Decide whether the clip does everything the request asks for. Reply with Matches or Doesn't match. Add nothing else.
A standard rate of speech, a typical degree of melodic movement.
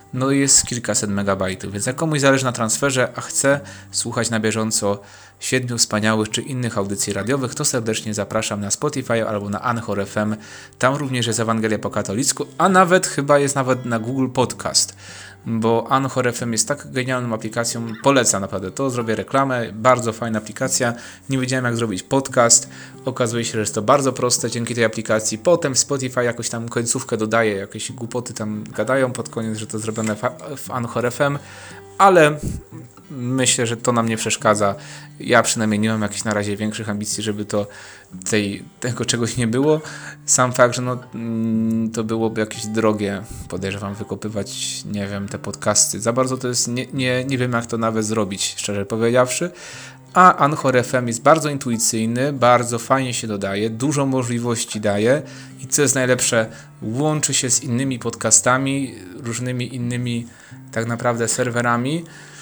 Doesn't match